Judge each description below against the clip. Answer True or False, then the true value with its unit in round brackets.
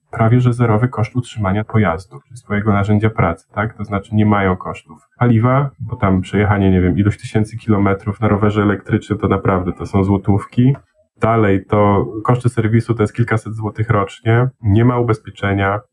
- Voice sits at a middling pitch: False (105 Hz)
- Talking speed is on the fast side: True (170 wpm)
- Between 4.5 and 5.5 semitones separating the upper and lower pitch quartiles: False (2.8 semitones)